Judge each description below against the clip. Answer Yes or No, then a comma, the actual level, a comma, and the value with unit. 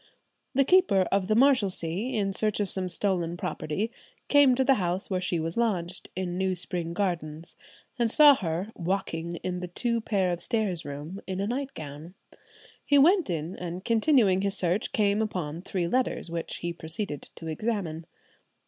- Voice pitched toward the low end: No, high, 190 Hz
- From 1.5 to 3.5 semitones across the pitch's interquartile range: No, average, 4.4 semitones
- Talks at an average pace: Yes, average, 165 wpm